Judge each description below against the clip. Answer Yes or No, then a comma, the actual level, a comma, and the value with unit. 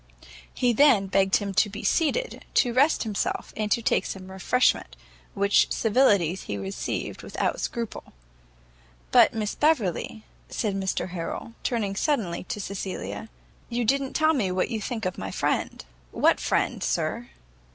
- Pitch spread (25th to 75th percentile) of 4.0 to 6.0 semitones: Yes, average, 4.3 semitones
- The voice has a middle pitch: No, high, 210 Hz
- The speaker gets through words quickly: No, average, 150 wpm